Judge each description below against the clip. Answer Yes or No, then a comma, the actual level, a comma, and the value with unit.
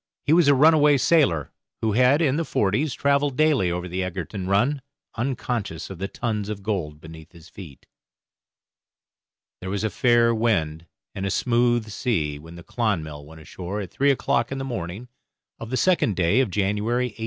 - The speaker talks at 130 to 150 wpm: No, average, 180 wpm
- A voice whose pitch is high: No, low, 110 Hz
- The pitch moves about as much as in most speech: No, wide, 6.4 semitones